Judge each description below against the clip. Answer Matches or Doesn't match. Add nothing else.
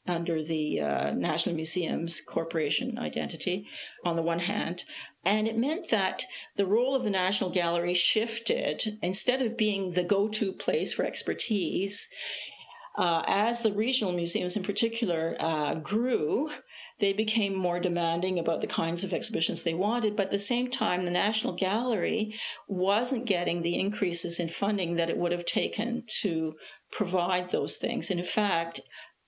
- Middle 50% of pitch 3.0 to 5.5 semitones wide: Matches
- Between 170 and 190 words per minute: Doesn't match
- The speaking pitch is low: Doesn't match